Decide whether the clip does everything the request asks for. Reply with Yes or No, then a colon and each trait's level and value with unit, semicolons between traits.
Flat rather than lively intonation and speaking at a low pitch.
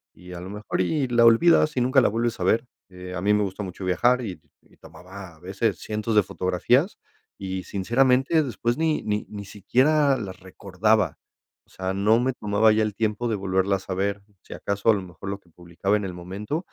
No: average, 4.1 semitones; low, 105 Hz